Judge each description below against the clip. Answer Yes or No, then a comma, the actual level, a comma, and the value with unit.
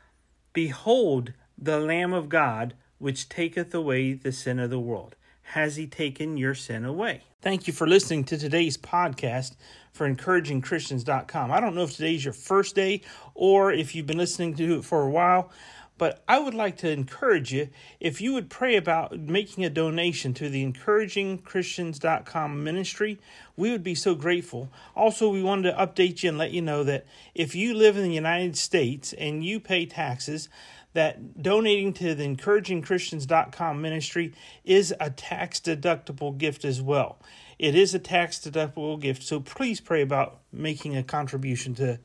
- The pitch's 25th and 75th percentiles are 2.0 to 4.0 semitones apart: No, average, 4.5 semitones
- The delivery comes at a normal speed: Yes, average, 170 wpm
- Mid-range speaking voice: Yes, medium, 160 Hz